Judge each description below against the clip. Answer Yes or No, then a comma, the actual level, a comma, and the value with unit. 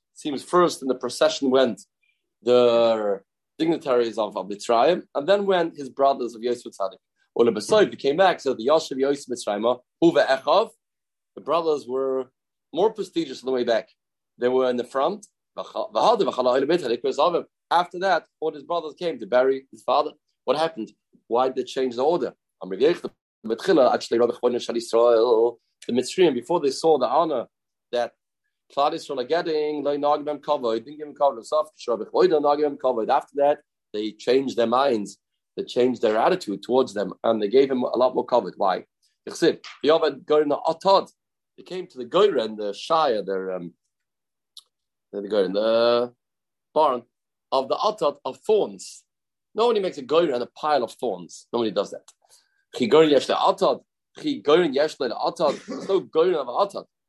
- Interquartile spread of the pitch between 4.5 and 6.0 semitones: Yes, wide, 5.6 semitones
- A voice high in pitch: No, low, 135 Hz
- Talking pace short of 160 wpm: No, average, 170 wpm